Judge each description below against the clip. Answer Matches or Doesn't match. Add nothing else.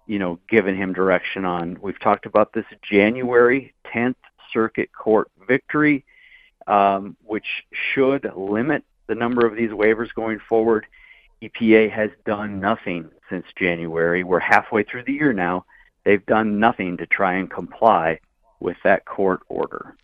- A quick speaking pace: Doesn't match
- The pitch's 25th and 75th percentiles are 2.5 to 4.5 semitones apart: Matches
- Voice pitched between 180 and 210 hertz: Doesn't match